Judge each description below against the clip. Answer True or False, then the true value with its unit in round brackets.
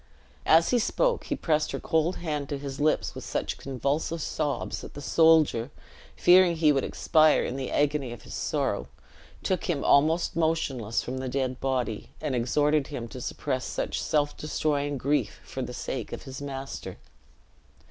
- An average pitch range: True (3.1 semitones)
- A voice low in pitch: False (145 Hz)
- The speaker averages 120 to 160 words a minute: False (170 wpm)